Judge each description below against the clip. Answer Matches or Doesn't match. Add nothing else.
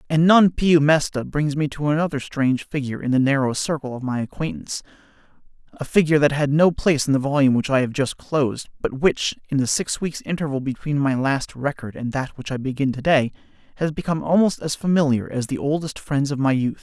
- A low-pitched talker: Doesn't match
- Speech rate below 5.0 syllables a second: Doesn't match